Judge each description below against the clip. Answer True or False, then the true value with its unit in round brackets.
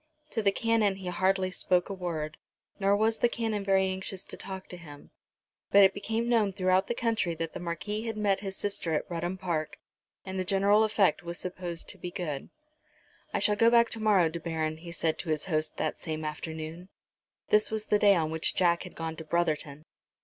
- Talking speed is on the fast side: True (210 wpm)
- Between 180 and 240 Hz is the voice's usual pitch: True (185 Hz)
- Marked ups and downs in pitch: False (3.7 semitones)